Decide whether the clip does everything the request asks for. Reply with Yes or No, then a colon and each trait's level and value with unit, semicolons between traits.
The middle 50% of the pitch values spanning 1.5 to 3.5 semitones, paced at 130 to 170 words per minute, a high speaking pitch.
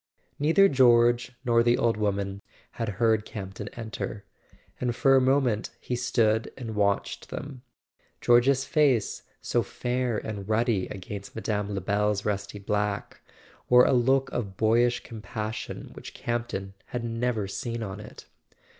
No: average, 2.9 semitones; average, 140 wpm; low, 115 Hz